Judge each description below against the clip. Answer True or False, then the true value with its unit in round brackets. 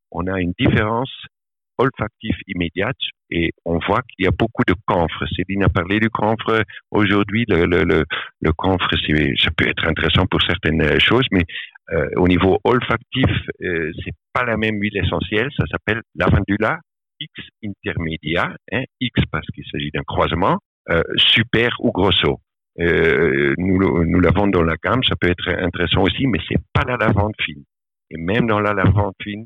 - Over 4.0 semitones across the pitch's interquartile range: False (3.7 semitones)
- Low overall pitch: True (95 Hz)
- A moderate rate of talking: True (175 wpm)